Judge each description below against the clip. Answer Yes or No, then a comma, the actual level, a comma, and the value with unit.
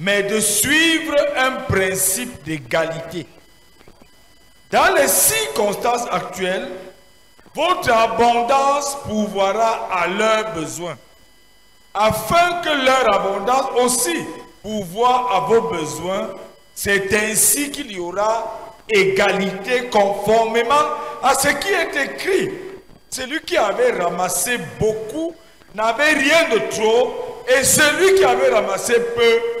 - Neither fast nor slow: No, slow, 105 wpm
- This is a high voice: Yes, high, 225 Hz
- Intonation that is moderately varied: No, wide, 6.8 semitones